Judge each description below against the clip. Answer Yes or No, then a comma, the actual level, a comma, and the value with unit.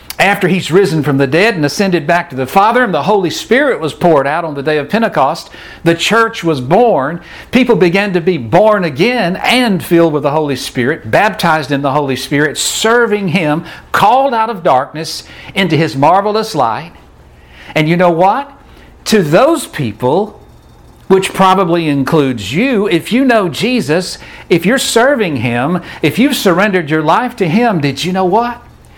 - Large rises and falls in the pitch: Yes, wide, 5.9 semitones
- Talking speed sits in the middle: Yes, average, 175 wpm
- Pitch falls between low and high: Yes, medium, 180 Hz